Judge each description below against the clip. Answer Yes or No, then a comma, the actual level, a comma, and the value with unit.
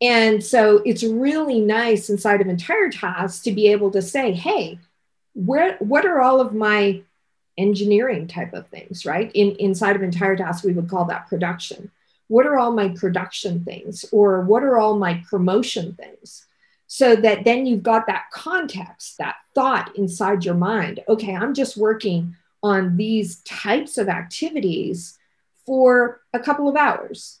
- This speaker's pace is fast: No, average, 165 wpm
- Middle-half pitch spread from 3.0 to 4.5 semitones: Yes, average, 3.9 semitones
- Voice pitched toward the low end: No, high, 210 Hz